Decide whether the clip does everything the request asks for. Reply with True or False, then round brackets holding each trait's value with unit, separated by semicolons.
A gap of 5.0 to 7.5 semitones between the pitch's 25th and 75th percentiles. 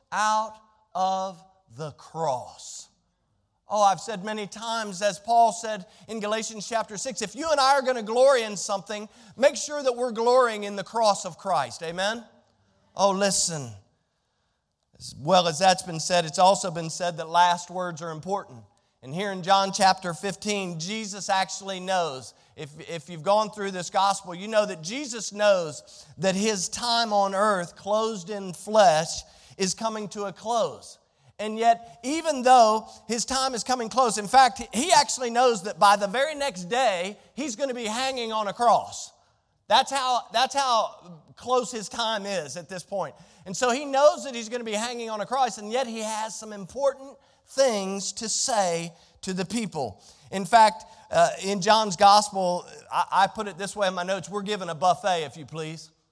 False (3.9 semitones)